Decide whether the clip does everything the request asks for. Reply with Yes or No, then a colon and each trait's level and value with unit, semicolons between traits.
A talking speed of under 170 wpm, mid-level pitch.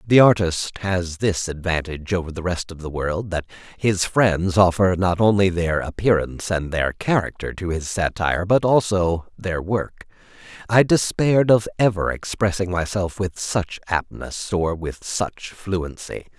No: average, 155 wpm; very low, 90 Hz